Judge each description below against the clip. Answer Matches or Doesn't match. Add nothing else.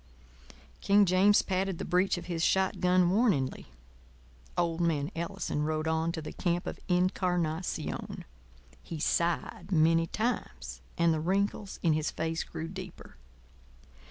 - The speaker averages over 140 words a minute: Doesn't match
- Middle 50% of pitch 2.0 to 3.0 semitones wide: Matches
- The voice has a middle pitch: Matches